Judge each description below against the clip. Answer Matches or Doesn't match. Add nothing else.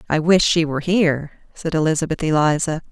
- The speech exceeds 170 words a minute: Doesn't match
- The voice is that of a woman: Matches